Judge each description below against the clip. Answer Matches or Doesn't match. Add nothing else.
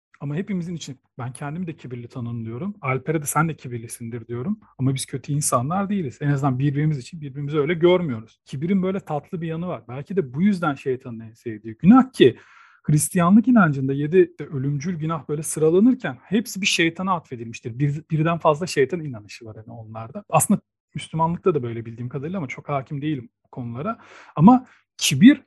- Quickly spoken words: Matches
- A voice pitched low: Doesn't match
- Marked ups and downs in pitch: Matches